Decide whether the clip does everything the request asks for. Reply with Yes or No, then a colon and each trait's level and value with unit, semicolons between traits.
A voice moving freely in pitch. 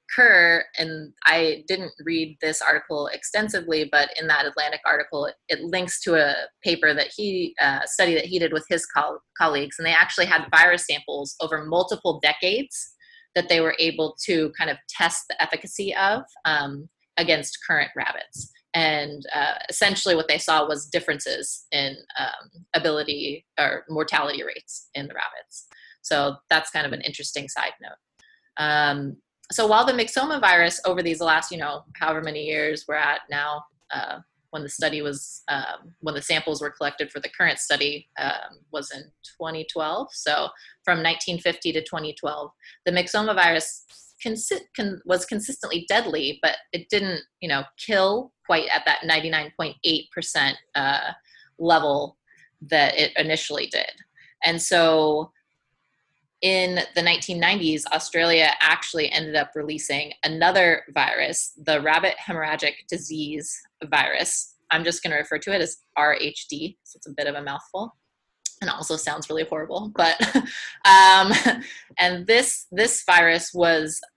No: average, 3.5 semitones